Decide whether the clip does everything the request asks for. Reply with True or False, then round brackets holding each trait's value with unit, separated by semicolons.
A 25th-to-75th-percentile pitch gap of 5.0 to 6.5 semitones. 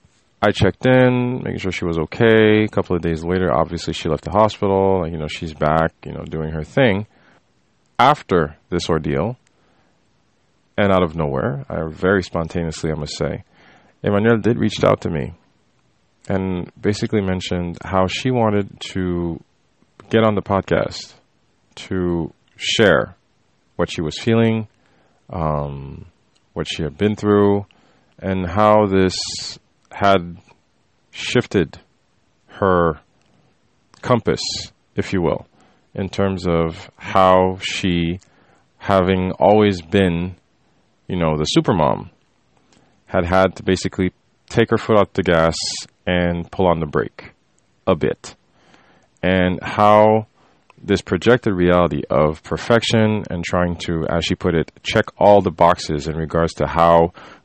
False (3.5 semitones)